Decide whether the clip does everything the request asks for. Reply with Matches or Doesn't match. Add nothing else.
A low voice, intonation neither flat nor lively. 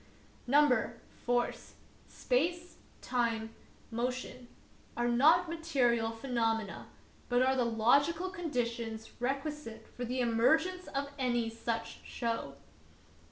Doesn't match